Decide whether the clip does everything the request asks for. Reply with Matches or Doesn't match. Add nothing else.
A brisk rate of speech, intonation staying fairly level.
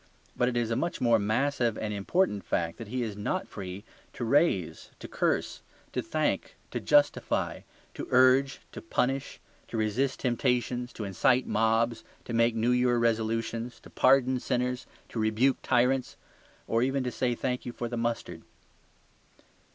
Doesn't match